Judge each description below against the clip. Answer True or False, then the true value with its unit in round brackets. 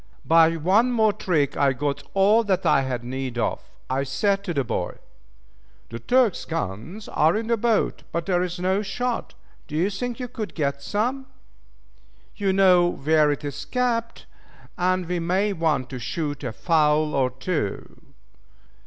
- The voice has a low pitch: False (170 Hz)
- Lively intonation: True (6.4 semitones)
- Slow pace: False (165 wpm)